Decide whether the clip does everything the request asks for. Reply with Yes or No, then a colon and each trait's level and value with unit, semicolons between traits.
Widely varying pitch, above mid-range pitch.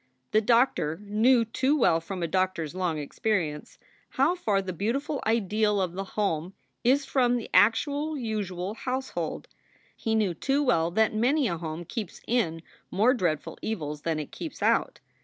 Yes: wide, 5.9 semitones; high, 210 Hz